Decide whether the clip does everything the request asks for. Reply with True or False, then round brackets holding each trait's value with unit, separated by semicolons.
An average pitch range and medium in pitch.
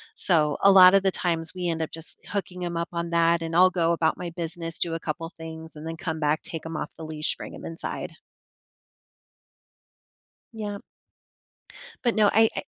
False (2.0 semitones; 170 Hz)